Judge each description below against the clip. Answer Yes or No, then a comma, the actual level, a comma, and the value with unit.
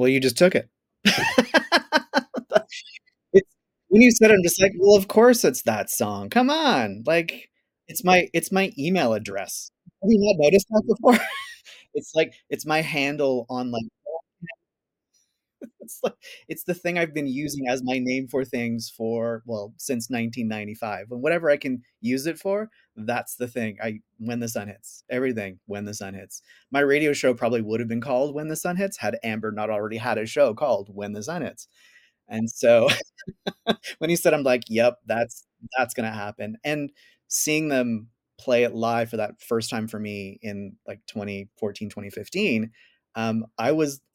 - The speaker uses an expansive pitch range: Yes, wide, 7.9 semitones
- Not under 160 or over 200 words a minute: Yes, average, 180 wpm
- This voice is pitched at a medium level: No, low, 130 Hz